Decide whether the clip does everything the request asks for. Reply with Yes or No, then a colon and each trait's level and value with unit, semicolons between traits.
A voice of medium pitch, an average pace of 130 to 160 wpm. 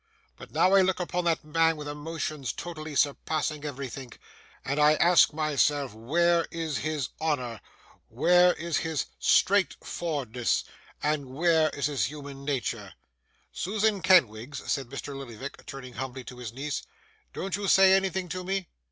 Yes: medium, 150 Hz; average, 150 wpm